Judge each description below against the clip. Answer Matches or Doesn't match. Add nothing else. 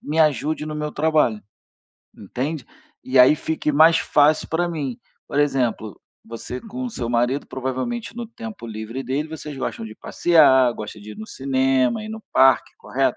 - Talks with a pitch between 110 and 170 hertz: Matches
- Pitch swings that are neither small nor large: Matches